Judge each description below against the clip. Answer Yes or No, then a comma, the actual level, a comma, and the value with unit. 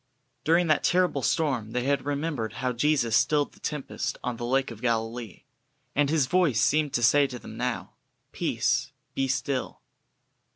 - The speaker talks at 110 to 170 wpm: Yes, average, 165 wpm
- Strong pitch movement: No, average, 3.8 semitones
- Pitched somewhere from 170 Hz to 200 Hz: No, low, 135 Hz